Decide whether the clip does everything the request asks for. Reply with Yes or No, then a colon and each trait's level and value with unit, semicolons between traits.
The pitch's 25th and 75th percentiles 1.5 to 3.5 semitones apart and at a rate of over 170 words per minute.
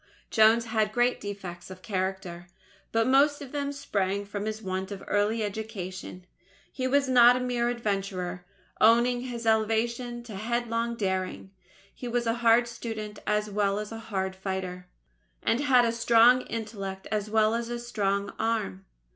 No: average, 3.2 semitones; average, 155 wpm